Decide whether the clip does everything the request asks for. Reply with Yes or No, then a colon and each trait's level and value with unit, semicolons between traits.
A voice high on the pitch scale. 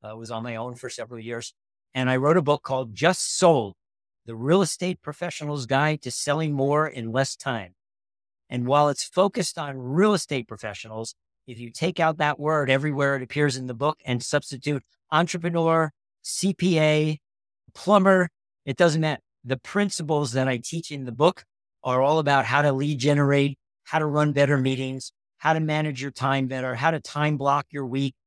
No: medium, 140 Hz